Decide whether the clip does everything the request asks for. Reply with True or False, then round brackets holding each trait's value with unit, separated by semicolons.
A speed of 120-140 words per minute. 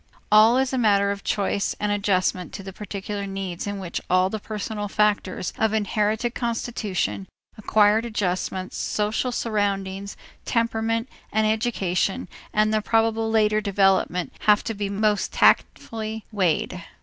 True (135 wpm)